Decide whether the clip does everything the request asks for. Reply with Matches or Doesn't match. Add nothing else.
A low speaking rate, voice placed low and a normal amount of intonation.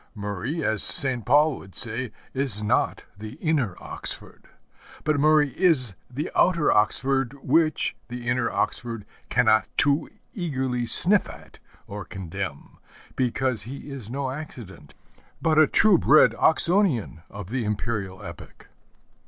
Doesn't match